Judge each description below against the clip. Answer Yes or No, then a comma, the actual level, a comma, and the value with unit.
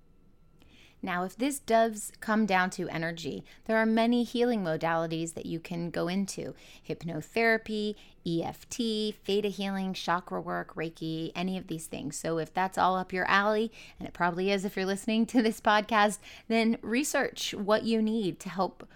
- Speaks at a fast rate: No, average, 170 wpm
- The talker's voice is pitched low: No, high, 195 Hz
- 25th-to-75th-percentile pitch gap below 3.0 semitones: No, average, 4.9 semitones